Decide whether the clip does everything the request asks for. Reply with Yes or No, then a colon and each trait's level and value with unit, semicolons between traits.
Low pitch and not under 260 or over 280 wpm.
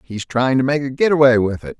Yes: low, 130 Hz; fast, 265 wpm